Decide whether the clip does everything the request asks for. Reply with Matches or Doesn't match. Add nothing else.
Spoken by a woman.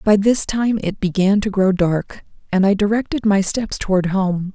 Matches